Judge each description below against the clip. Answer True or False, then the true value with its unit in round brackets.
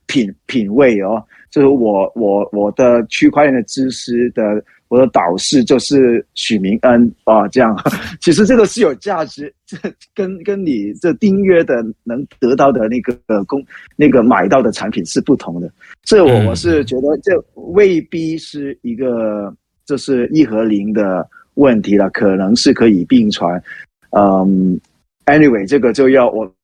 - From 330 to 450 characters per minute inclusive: False (235 characters per minute)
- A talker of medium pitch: False (125 Hz)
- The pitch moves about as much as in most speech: False (6.2 semitones)